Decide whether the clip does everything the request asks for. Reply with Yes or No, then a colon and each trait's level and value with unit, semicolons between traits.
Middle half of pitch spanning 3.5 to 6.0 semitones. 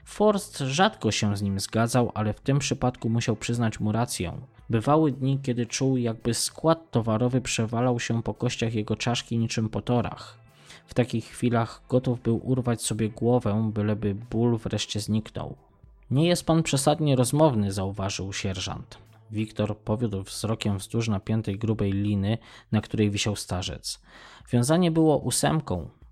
No: average, 2.8 semitones